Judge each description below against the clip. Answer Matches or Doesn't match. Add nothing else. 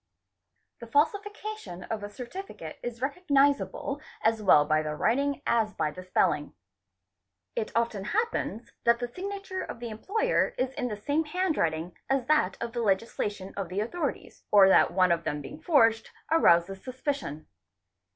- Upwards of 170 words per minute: Doesn't match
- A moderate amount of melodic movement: Doesn't match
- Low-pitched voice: Doesn't match